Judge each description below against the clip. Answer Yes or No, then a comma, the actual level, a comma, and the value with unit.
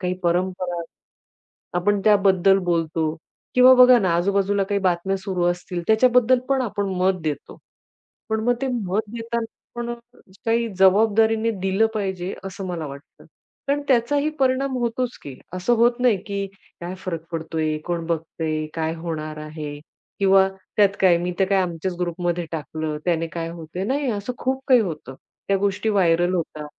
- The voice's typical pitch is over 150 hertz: Yes, high, 190 Hz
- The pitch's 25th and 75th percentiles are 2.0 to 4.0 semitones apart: No, average, 4.7 semitones